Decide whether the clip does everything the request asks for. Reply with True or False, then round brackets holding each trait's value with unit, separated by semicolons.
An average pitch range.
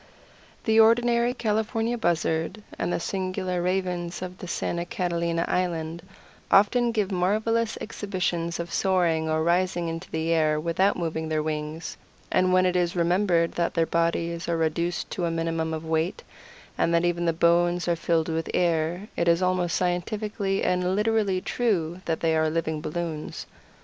False (2.3 semitones)